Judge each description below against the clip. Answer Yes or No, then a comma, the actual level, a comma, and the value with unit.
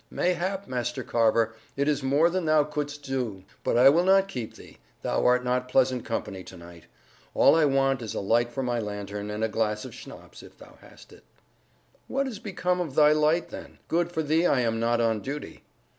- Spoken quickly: Yes, fast, 210 wpm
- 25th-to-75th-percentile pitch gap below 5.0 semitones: No, wide, 5.6 semitones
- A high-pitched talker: No, low, 130 Hz